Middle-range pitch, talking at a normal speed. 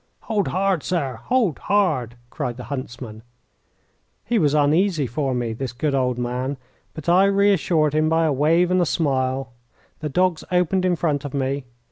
Yes: medium, 150 Hz; average, 170 wpm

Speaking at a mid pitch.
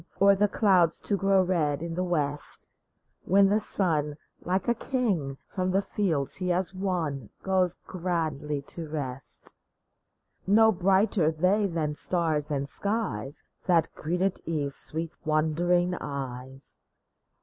Yes: medium, 175 Hz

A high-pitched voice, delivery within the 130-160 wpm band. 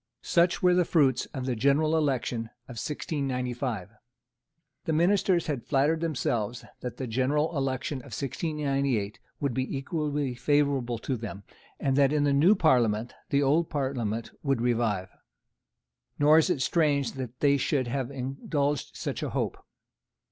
No: low, 135 Hz; average, 150 wpm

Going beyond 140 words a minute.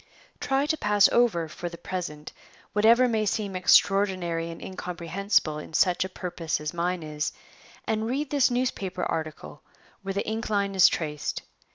Yes: average, 160 wpm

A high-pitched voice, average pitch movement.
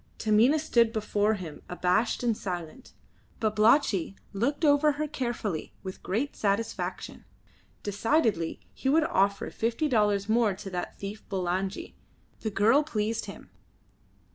Yes: high, 215 Hz; average, 3.9 semitones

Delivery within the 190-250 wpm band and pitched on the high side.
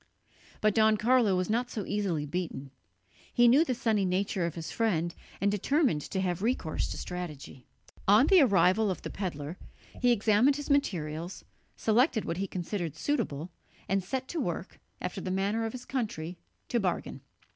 No: average, 170 wpm; high, 200 Hz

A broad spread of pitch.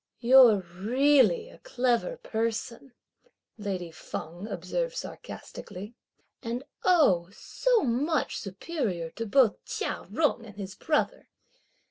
Yes: wide, 7.0 semitones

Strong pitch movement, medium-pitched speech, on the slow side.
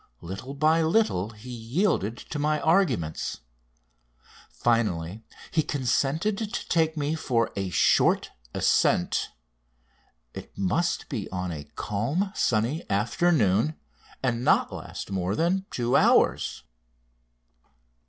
No: wide, 8.1 semitones; low, 125 Hz; slow, 110 wpm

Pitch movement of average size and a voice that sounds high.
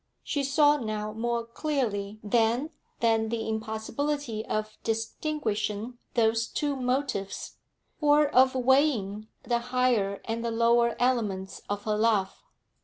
Yes: average, 3.2 semitones; high, 230 Hz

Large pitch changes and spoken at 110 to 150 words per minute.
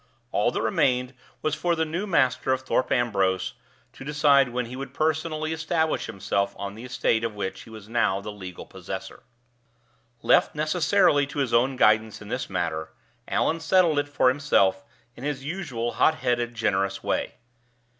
No: wide, 6.2 semitones; average, 170 wpm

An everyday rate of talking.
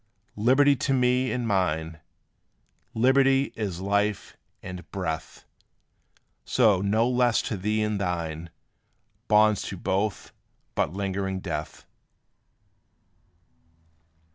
No: slow, 95 wpm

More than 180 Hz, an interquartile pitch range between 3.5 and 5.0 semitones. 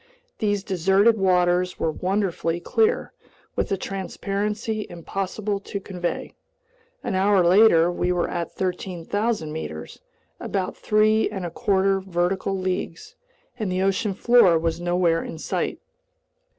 No: high, 190 Hz; narrow, 2.6 semitones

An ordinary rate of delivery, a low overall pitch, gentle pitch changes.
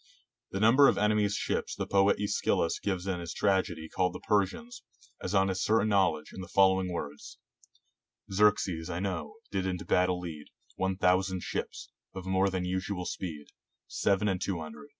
Yes: average, 180 wpm; very low, 95 Hz; narrow, 1.9 semitones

